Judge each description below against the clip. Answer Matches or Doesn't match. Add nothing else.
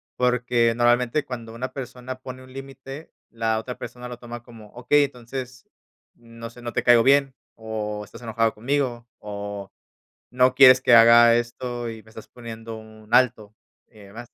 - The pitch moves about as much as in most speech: Doesn't match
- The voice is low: Matches